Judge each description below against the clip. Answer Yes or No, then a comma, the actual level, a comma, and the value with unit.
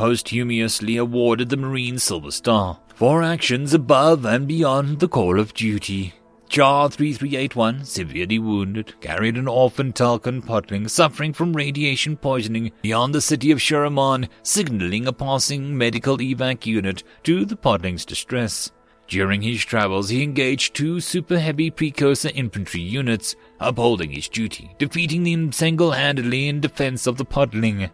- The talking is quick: No, slow, 135 wpm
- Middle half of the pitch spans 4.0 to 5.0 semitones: Yes, average, 4.6 semitones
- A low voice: Yes, low, 125 Hz